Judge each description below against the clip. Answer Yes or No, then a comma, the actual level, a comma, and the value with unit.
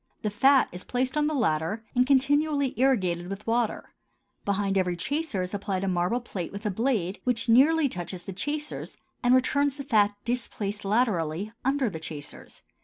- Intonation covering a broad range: Yes, wide, 6.1 semitones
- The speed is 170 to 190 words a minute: Yes, average, 175 wpm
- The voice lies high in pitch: Yes, high, 220 Hz